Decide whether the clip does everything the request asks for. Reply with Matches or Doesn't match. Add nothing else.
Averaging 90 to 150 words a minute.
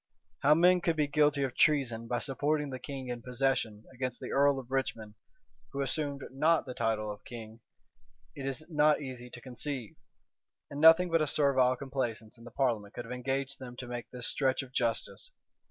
Doesn't match